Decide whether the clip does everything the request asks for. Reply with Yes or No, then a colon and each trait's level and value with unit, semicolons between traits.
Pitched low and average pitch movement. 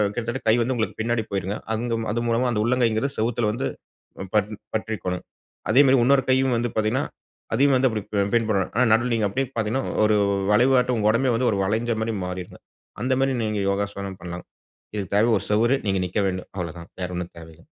Yes: low, 110 Hz; average, 3.6 semitones